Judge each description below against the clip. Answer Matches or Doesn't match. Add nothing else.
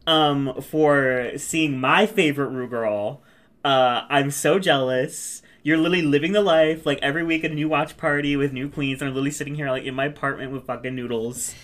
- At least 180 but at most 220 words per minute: Matches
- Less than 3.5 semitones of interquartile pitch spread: Matches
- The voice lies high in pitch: Doesn't match